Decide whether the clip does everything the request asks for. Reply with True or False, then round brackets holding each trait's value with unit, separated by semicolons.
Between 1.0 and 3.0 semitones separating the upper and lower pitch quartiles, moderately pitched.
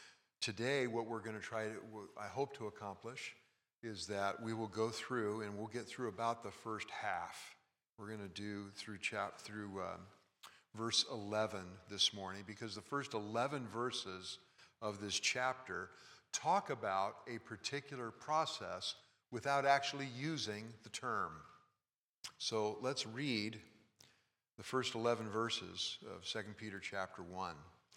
False (2.5 semitones; 110 Hz)